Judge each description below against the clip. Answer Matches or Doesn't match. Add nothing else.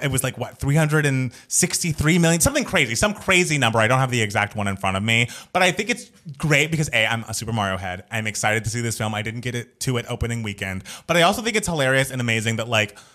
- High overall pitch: Doesn't match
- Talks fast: Matches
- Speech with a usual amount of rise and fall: Doesn't match